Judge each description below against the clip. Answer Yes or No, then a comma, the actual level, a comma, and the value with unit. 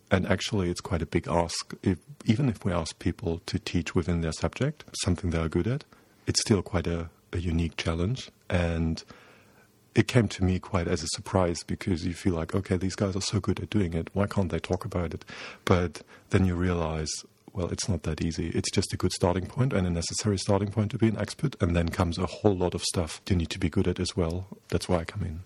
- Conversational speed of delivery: No, fast, 245 wpm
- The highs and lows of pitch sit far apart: No, average, 3.3 semitones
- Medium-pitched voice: No, very low, 90 Hz